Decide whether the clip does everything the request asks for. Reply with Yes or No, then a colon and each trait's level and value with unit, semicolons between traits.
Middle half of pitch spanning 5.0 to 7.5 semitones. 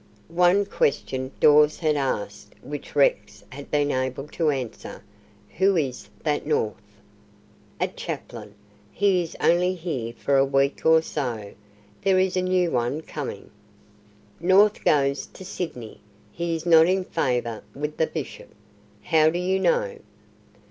Yes: average, 5.3 semitones